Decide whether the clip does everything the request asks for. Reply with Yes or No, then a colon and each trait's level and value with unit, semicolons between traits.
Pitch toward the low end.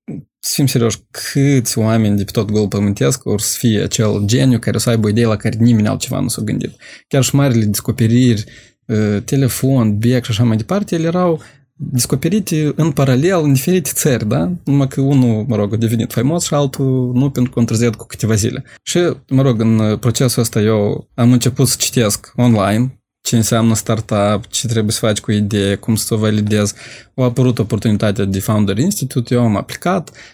Yes: low, 120 Hz